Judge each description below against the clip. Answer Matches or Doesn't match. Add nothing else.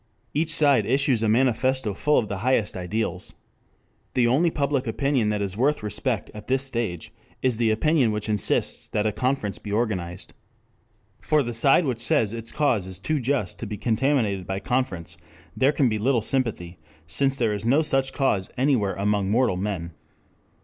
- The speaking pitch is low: Matches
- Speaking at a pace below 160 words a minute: Doesn't match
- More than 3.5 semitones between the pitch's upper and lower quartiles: Matches